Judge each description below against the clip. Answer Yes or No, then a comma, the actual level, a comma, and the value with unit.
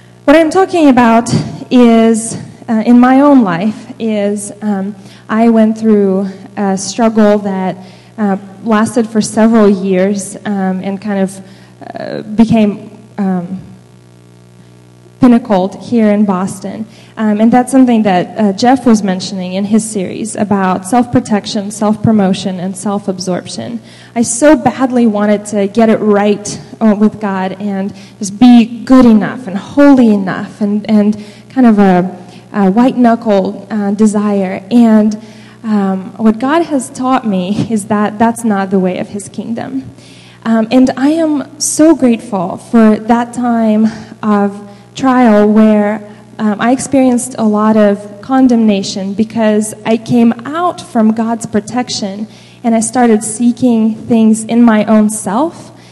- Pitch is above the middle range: Yes, high, 215 Hz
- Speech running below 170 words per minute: Yes, average, 140 wpm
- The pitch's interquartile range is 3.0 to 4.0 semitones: No, narrow, 2.6 semitones